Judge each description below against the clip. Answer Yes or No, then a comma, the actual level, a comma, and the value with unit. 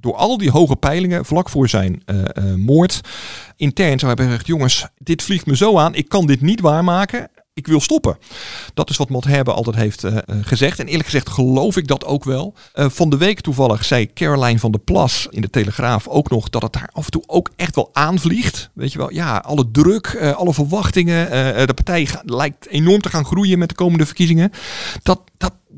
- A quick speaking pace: Yes, fast, 220 wpm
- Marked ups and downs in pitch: Yes, wide, 5.8 semitones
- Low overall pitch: No, medium, 145 Hz